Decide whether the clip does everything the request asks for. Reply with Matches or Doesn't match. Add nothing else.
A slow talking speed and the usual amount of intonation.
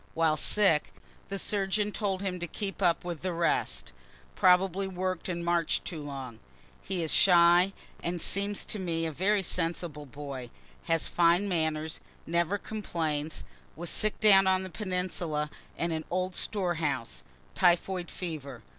Doesn't match